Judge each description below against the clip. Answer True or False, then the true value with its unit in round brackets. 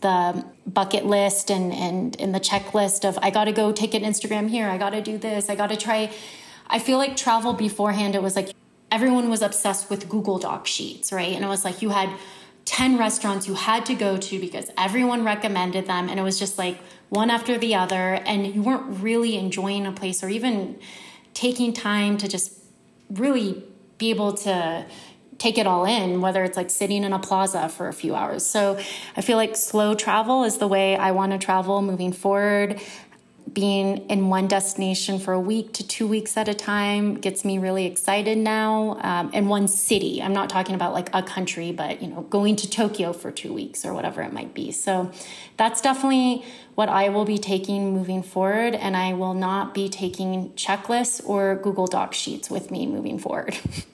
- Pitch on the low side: False (200 Hz)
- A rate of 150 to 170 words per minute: False (200 wpm)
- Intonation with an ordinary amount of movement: False (2.3 semitones)